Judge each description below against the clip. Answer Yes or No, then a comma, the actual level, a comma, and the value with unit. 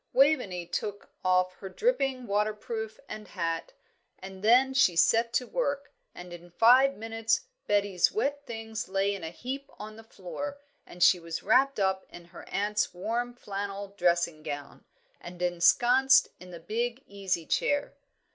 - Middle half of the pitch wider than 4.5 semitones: Yes, average, 5.2 semitones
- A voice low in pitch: No, high, 210 Hz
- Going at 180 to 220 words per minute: No, average, 155 wpm